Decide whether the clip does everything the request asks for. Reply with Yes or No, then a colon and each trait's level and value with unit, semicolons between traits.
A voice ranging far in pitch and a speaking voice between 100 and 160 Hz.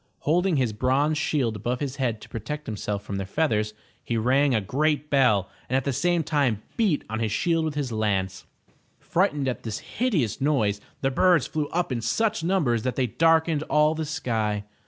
Yes: wide, 5.9 semitones; low, 135 Hz